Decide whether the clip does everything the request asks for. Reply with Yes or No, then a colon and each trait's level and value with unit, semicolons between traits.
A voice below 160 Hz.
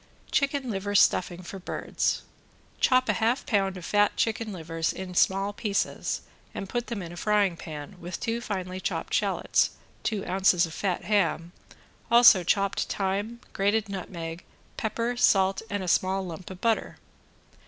No: high, 195 Hz